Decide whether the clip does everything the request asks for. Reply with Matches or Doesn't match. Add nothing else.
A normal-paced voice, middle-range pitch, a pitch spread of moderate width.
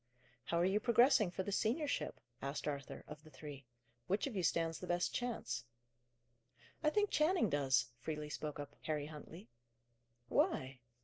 Doesn't match